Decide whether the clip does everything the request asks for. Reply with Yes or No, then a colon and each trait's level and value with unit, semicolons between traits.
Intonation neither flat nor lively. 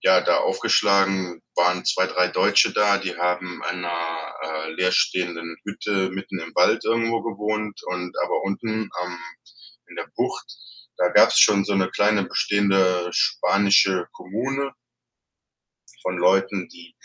No: narrow, 2.3 semitones